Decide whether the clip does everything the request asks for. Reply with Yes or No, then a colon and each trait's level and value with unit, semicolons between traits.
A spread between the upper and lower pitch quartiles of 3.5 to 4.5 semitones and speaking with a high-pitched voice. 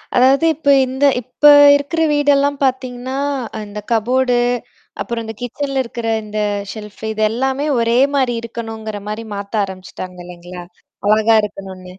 Yes: average, 3.8 semitones; high, 230 Hz